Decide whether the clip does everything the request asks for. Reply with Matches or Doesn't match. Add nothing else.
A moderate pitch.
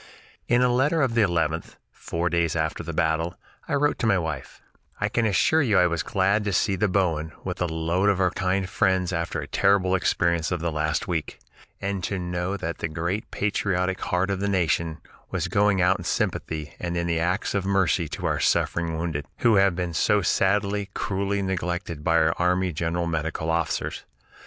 Doesn't match